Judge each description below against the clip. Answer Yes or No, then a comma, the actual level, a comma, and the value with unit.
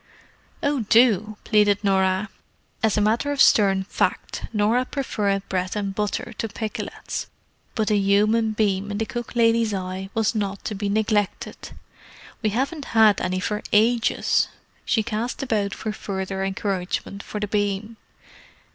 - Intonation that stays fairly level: Yes, narrow, 2.2 semitones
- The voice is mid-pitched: No, high, 210 Hz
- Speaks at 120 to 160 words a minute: Yes, average, 145 wpm